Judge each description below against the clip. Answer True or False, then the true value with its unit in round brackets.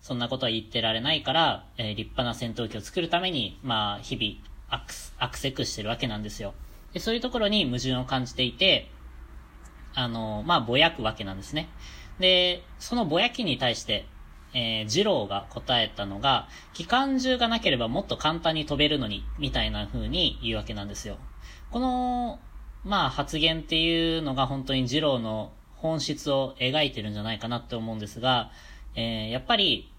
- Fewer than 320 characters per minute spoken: False (360 characters per minute)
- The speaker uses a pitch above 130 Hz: False (120 Hz)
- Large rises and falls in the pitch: True (6.4 semitones)